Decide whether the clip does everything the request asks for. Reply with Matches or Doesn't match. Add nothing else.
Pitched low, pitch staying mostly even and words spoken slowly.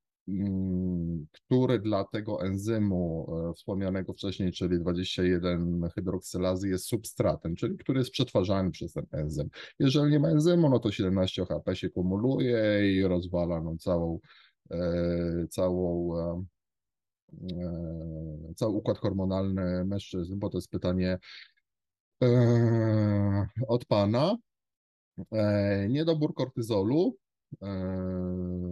Doesn't match